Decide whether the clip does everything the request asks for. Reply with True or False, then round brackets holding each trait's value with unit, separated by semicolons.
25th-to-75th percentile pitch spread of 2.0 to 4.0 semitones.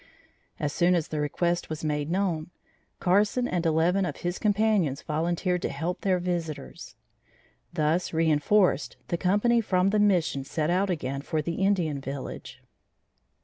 True (3.6 semitones)